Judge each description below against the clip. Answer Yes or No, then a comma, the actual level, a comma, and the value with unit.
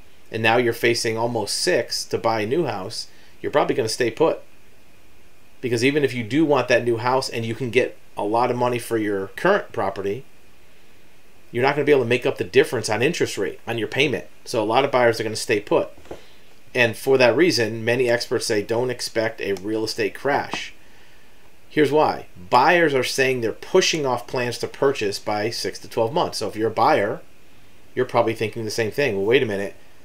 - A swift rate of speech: Yes, fast, 220 wpm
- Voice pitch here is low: Yes, low, 120 Hz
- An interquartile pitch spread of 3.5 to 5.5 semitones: No, narrow, 2.6 semitones